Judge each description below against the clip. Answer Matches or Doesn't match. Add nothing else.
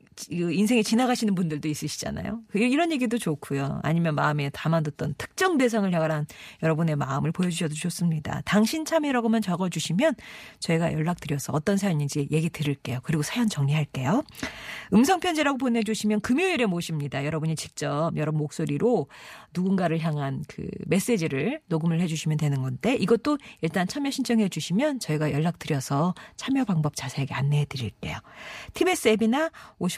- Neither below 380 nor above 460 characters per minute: Matches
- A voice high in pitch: Doesn't match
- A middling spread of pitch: Doesn't match